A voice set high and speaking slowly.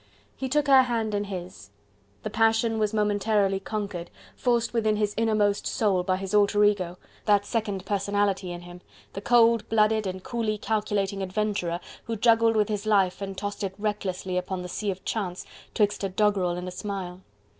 No: high, 205 Hz; average, 180 wpm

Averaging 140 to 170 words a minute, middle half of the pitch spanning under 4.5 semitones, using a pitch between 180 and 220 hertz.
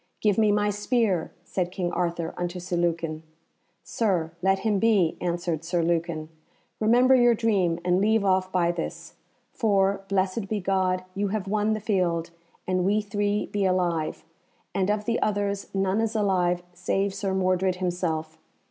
Yes: average, 160 wpm; average, 2.8 semitones; high, 190 Hz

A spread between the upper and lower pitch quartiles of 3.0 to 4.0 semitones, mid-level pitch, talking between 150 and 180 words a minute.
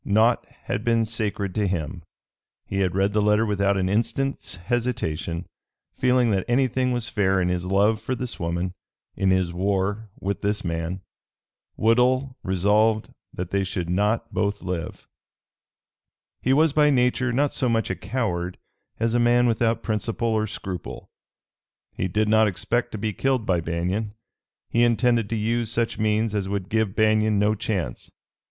No: average, 3.5 semitones; low, 105 Hz; average, 160 wpm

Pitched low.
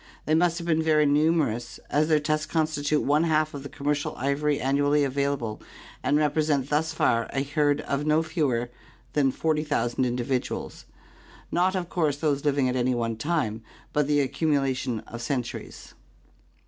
No: medium, 145 Hz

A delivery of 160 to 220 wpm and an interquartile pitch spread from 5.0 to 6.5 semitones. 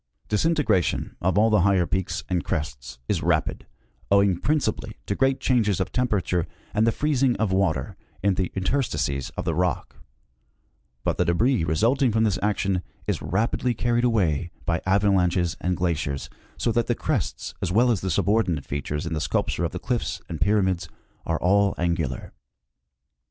No: average, 170 wpm; average, 4.6 semitones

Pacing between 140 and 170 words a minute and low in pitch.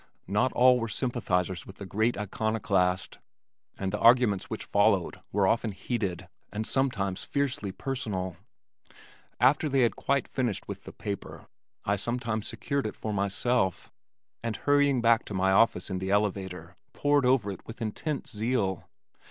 Yes: average, 150 wpm; low, 110 Hz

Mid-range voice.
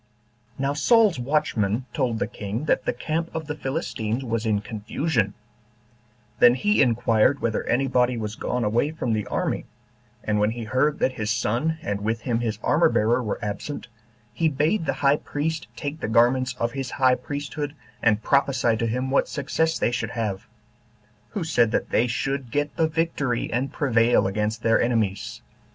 No: low, 125 Hz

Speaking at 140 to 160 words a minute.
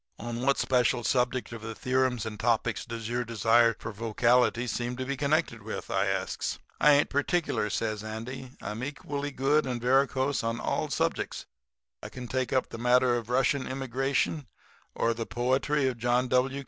No: average, 180 wpm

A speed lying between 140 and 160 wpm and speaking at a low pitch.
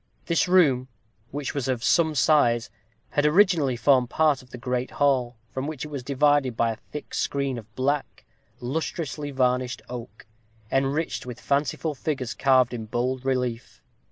Yes: average, 155 wpm; low, 130 Hz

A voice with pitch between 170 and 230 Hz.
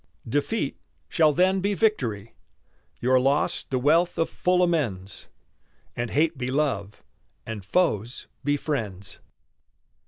No: medium, 140 Hz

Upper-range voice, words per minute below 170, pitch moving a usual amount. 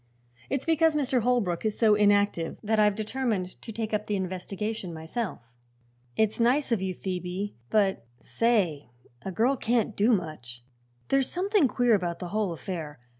Yes: high, 210 Hz; average, 160 wpm; average, 4.7 semitones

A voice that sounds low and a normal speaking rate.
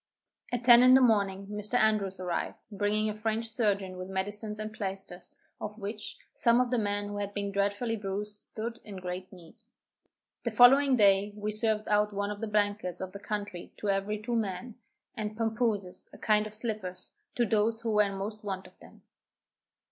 No: high, 210 Hz; average, 190 wpm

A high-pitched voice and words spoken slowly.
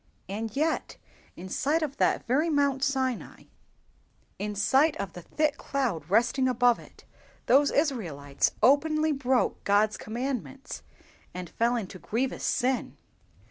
Yes: very high, 255 Hz; slow, 130 wpm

